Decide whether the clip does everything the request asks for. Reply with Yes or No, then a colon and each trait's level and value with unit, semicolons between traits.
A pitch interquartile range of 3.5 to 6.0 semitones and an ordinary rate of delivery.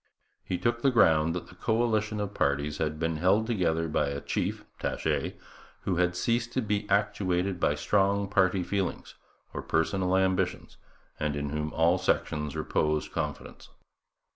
Yes: average, 4.5 semitones; average, 155 wpm